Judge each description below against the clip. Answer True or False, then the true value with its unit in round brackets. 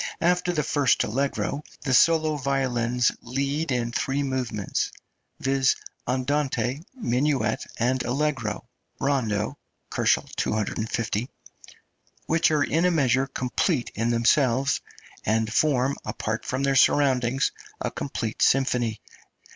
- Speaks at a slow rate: True (110 wpm)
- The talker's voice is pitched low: True (130 Hz)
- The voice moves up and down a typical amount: True (3.1 semitones)